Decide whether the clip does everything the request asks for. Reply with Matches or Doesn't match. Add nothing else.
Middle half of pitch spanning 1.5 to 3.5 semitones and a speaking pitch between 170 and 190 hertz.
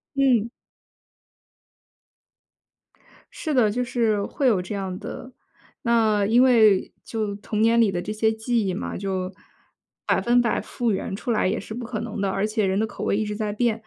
Doesn't match